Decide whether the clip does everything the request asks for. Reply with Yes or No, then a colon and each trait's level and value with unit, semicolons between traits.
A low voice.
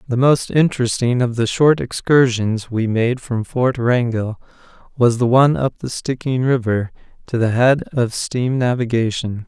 Yes: low, 120 Hz